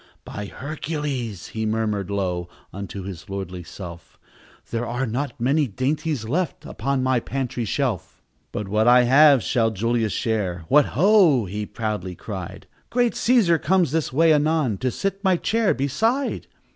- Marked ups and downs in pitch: Yes, wide, 6.6 semitones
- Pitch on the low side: Yes, low, 125 Hz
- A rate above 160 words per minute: No, average, 150 wpm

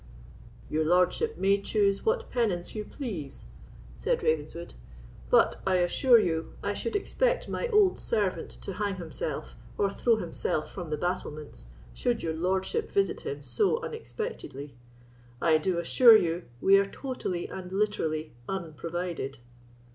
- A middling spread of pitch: No, wide, 6.3 semitones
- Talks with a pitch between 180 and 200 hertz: Yes, high, 190 Hz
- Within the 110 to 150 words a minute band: Yes, average, 140 wpm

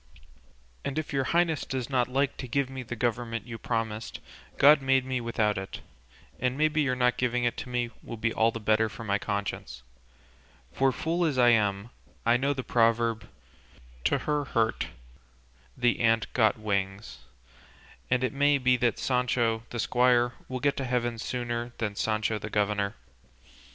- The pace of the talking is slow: No, average, 170 wpm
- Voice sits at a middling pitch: No, low, 120 Hz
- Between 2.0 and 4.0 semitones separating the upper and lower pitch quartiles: Yes, narrow, 2.6 semitones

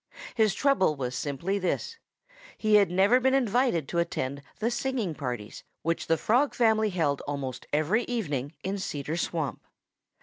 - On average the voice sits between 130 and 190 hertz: Yes, medium, 185 Hz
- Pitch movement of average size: No, wide, 7.6 semitones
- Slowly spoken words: No, average, 155 wpm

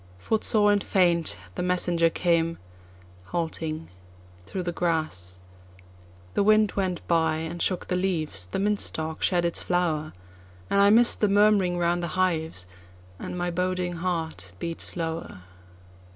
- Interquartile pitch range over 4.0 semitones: No, average, 2.8 semitones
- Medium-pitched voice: Yes, medium, 170 Hz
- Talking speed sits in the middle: No, slow, 130 wpm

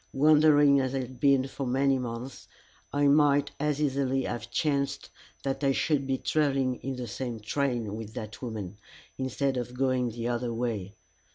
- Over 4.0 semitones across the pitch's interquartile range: No, narrow, 2.6 semitones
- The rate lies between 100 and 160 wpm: No, average, 170 wpm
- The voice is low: Yes, low, 130 Hz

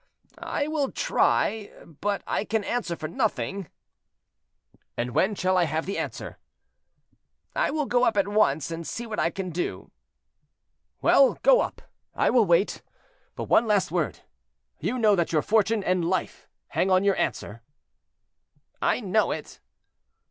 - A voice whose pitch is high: Yes, high, 200 Hz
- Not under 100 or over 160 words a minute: Yes, average, 155 wpm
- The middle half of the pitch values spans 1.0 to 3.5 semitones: No, average, 4.6 semitones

